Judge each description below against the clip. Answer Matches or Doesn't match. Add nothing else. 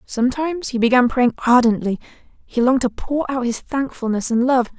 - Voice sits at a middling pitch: Doesn't match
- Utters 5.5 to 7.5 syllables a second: Matches